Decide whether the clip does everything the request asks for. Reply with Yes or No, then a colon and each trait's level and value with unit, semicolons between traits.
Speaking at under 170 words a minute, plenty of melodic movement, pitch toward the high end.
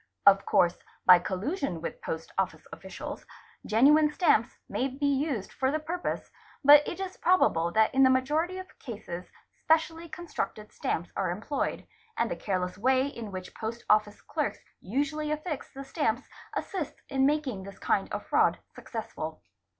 Yes: average, 160 wpm; wide, 7.0 semitones; very high, 265 Hz